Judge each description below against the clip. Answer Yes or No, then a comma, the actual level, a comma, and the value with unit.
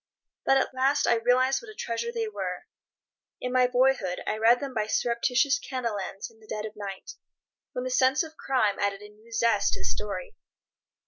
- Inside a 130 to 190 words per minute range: No, fast, 205 wpm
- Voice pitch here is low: No, high, 245 Hz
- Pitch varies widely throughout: No, average, 3.8 semitones